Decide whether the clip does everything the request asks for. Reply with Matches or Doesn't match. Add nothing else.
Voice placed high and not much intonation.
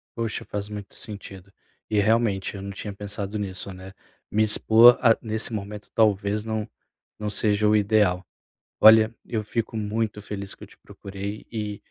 Doesn't match